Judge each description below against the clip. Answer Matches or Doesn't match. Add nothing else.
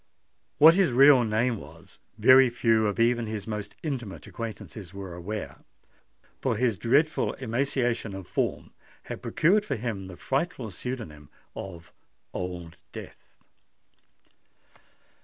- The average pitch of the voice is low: Matches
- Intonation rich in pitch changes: Doesn't match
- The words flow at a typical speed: Doesn't match